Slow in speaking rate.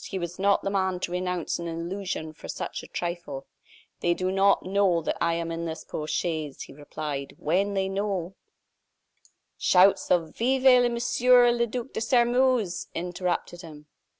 No: average, 170 wpm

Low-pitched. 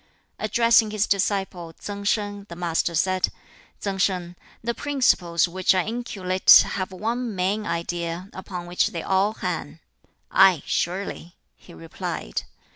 No: high, 190 Hz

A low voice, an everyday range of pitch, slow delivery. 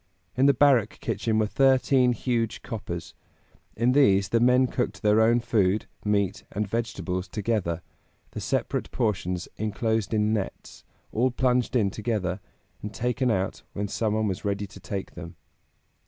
No: low, 110 Hz; average, 3.3 semitones; average, 155 wpm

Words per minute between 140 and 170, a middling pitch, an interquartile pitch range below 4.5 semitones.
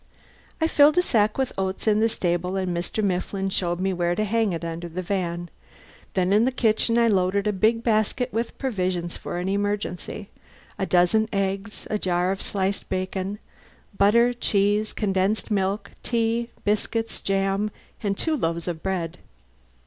No: average, 165 wpm; high, 195 Hz; average, 2.9 semitones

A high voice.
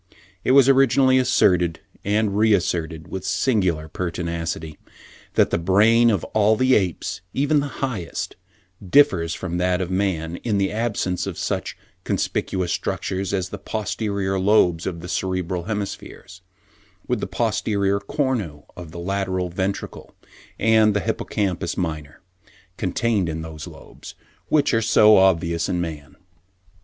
No: very low, 95 Hz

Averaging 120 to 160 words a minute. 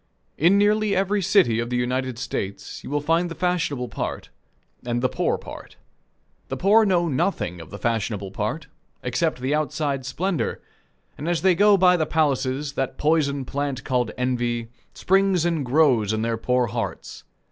No: average, 170 wpm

